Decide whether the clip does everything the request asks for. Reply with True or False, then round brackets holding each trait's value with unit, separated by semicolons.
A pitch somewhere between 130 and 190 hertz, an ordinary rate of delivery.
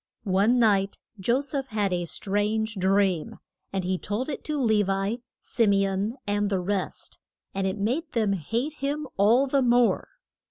False (205 Hz; 170 wpm)